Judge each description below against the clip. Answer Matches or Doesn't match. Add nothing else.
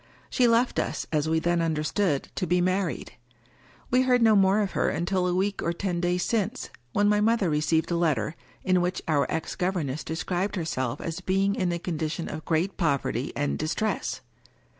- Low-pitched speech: Doesn't match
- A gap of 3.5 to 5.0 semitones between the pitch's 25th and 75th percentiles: Matches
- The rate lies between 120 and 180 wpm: Doesn't match